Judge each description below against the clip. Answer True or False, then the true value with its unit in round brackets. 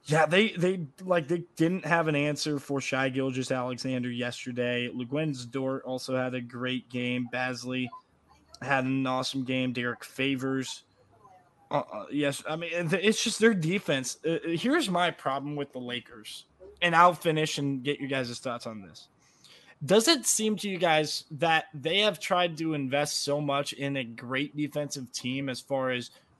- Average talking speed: True (170 wpm)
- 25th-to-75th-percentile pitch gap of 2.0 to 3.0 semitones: False (4.4 semitones)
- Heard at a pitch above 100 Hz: True (140 Hz)